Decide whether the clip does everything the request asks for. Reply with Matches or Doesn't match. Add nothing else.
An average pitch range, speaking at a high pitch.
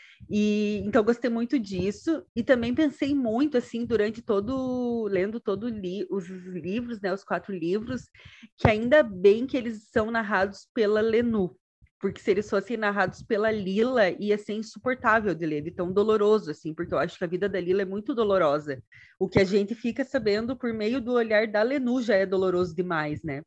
Matches